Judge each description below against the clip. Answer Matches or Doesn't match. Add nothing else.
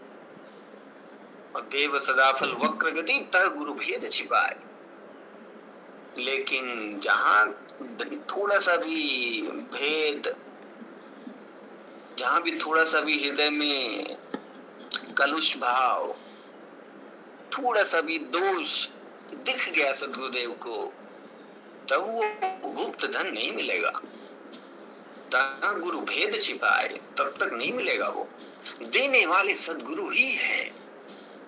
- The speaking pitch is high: Matches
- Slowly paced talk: Matches